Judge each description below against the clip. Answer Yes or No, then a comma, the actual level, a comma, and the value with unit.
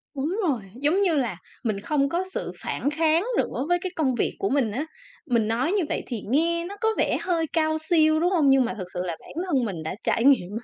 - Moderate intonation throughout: No, wide, 5.9 semitones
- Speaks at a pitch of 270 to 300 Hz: Yes, very high, 285 Hz